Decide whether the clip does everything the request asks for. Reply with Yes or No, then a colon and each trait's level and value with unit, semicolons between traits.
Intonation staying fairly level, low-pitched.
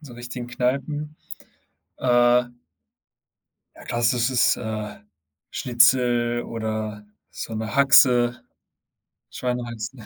Yes: narrow, 1.4 semitones; low, 120 Hz